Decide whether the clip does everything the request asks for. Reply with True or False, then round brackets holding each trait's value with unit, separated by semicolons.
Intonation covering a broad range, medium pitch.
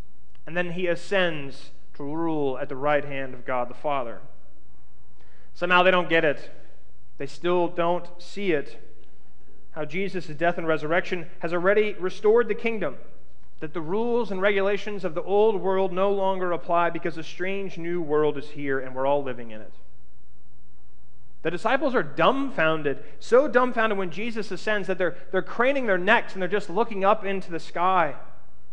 True (5.9 semitones; 170 Hz)